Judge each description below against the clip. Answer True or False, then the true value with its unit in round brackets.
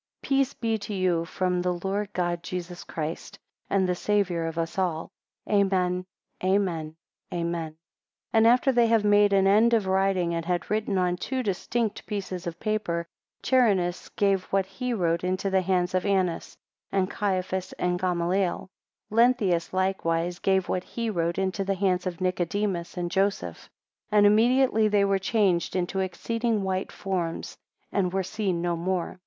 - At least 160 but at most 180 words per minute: True (165 wpm)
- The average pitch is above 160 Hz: True (190 Hz)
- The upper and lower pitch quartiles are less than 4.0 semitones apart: True (2.6 semitones)